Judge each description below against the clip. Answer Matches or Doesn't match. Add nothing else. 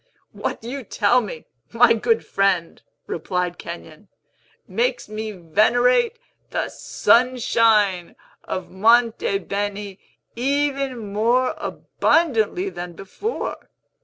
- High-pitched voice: Matches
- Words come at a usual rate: Doesn't match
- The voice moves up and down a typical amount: Matches